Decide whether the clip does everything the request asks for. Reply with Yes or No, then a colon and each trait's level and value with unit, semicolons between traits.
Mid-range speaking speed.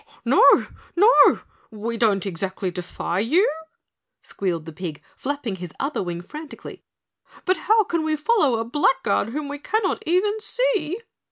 Yes: average, 145 wpm